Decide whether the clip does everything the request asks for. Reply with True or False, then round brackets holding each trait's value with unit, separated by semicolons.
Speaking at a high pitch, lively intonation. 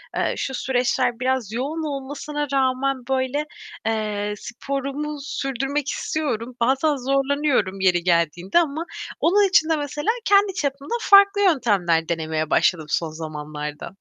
True (265 Hz; 6.5 semitones)